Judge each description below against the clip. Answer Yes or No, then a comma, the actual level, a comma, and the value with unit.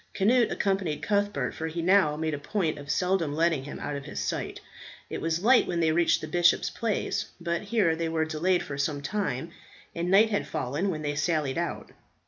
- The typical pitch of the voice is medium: Yes, medium, 170 Hz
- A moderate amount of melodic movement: Yes, average, 4.1 semitones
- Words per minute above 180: Yes, fast, 205 wpm